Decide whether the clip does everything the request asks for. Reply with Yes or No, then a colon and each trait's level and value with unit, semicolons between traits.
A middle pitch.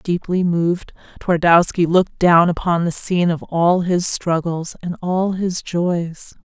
Yes: medium, 175 Hz